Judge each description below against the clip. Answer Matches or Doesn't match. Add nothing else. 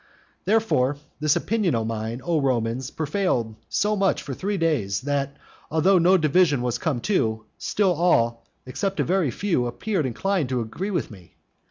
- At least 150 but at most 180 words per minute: Matches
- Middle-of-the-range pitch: Matches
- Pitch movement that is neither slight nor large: Doesn't match